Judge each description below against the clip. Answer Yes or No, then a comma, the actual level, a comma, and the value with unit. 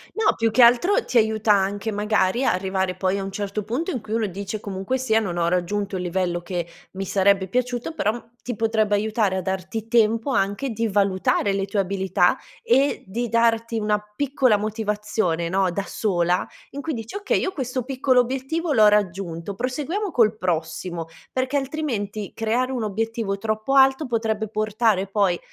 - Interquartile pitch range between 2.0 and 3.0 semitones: No, average, 3.9 semitones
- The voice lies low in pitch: No, high, 215 Hz